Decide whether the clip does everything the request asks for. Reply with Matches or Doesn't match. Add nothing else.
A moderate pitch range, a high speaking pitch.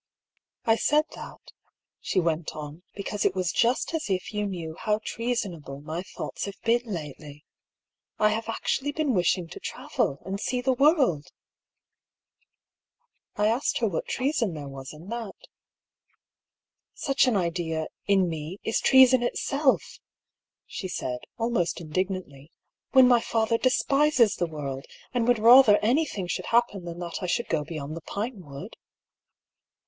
Doesn't match